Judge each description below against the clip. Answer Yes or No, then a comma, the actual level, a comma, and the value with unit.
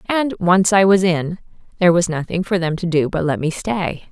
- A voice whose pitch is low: No, medium, 180 Hz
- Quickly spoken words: Yes, fast, 235 wpm